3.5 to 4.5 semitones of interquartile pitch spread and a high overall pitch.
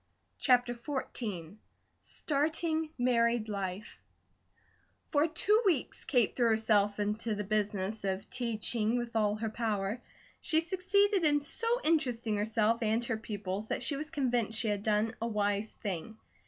Yes: average, 4.0 semitones; high, 230 Hz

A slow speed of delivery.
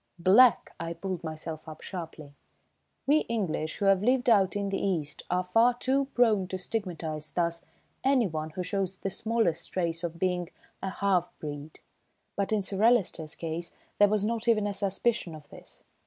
No: average, 170 wpm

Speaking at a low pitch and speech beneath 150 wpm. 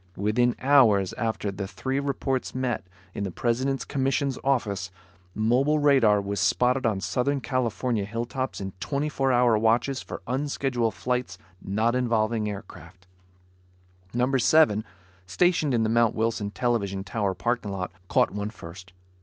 Yes: low, 120 Hz; average, 140 wpm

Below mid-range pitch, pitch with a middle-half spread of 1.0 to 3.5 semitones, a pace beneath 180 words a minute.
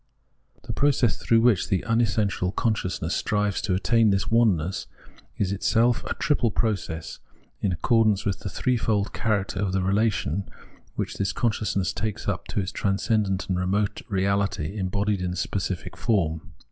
Yes: low, 100 Hz; average, 2.8 semitones; average, 150 wpm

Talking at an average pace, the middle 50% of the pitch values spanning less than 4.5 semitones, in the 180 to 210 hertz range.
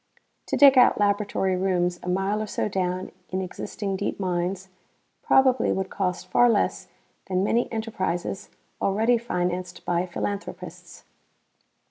No: slow, 130 wpm; narrow, 2.6 semitones; high, 190 Hz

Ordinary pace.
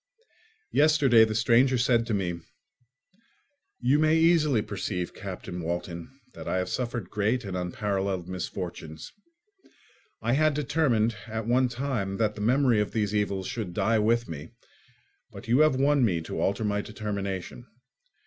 Yes: average, 150 wpm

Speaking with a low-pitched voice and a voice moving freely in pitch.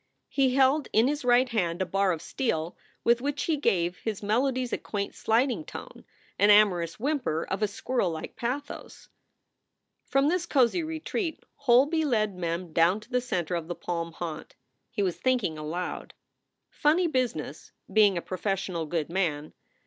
No: high, 215 Hz; wide, 7.2 semitones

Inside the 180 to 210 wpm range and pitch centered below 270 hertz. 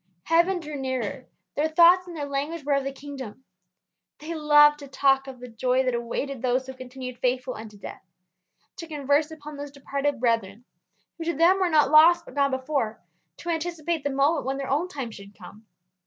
No: average, 195 wpm; very high, 280 Hz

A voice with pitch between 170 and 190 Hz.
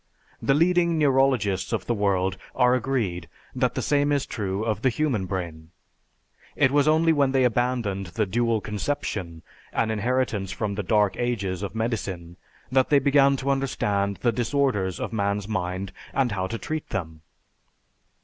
No: low, 110 Hz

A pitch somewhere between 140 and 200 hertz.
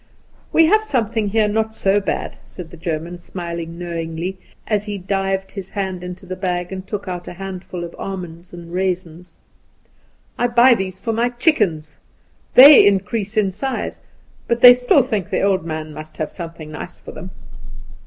Yes: high, 190 Hz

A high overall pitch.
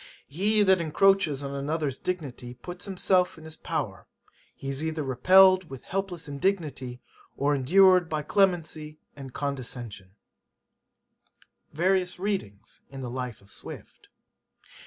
No: medium, 155 Hz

